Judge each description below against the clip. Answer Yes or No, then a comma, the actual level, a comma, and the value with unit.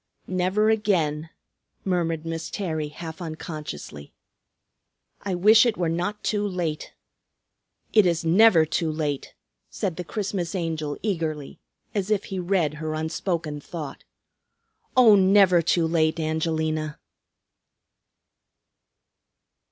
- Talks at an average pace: No, slow, 115 wpm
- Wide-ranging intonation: No, average, 3.5 semitones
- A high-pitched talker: No, medium, 165 Hz